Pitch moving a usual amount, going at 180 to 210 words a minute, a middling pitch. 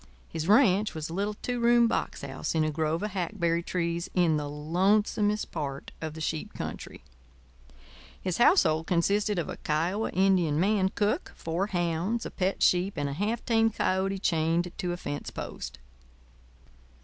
No: average, 4.2 semitones; average, 165 wpm; medium, 180 Hz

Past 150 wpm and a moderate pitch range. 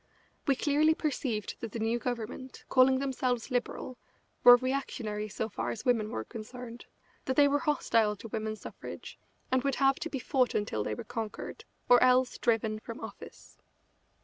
Yes: average, 170 wpm; average, 3.2 semitones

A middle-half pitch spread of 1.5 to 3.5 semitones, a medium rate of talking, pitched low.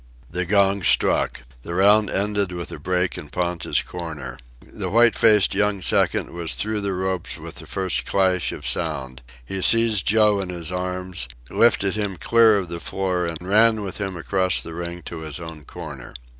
Yes: average, 2.8 semitones; average, 185 wpm; very low, 95 Hz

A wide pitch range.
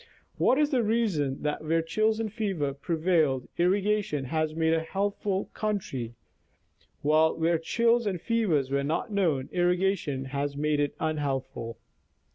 Yes: wide, 5.9 semitones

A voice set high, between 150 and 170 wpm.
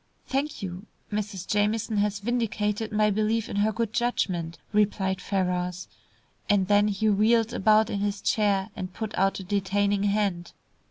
Yes: high, 205 Hz; average, 155 wpm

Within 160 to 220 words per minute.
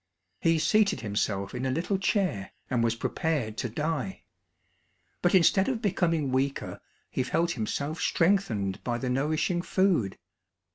No: average, 140 wpm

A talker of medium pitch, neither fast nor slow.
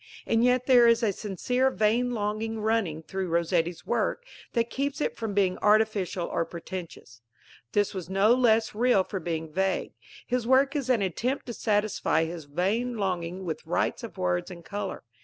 No: high, 205 Hz; average, 175 wpm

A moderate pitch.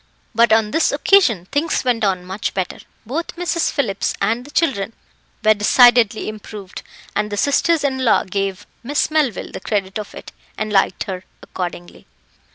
No: high, 215 Hz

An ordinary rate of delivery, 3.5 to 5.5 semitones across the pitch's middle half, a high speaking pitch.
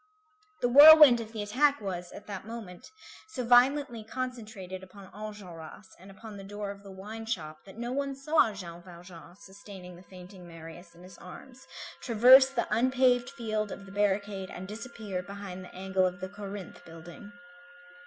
Yes: average, 170 wpm; average, 4.2 semitones; high, 200 Hz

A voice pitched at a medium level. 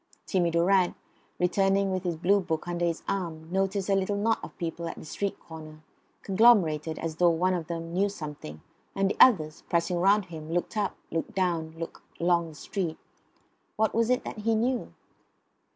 Yes: medium, 175 Hz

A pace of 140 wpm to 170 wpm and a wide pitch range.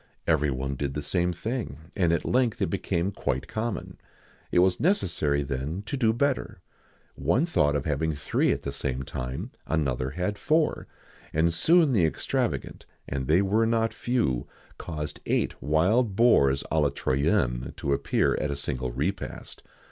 Yes: average, 165 wpm; wide, 7.7 semitones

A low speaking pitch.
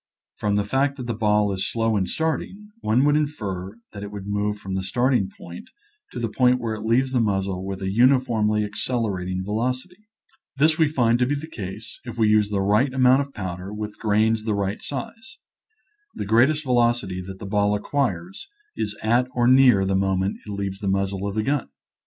Yes: low, 110 Hz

